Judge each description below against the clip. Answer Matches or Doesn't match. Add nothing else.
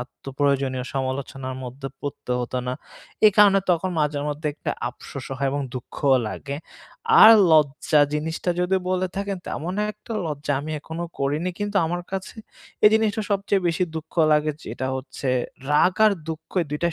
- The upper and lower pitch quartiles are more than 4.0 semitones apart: Matches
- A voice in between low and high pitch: Matches